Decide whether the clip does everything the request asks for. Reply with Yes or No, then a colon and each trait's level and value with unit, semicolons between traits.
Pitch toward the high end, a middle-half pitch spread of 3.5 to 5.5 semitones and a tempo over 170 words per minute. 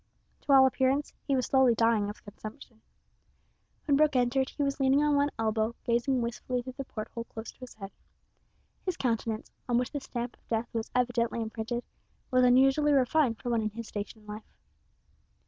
No: high, 245 Hz; average, 3.0 semitones; average, 190 wpm